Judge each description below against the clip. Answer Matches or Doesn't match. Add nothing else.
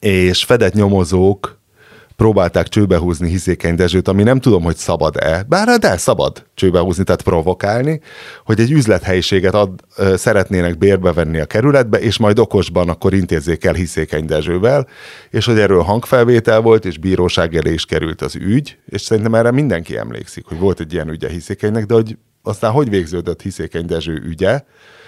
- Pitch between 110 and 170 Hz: Doesn't match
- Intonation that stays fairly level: Doesn't match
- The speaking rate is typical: Doesn't match